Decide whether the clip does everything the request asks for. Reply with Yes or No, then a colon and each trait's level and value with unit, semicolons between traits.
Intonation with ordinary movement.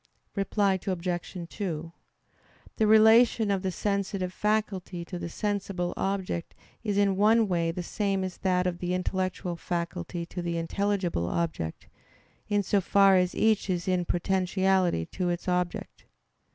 No: narrow, 2.3 semitones